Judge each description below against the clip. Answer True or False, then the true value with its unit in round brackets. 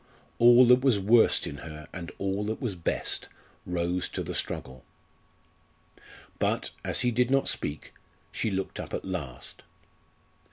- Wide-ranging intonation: True (6.0 semitones)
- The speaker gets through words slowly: False (150 wpm)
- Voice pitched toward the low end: True (95 Hz)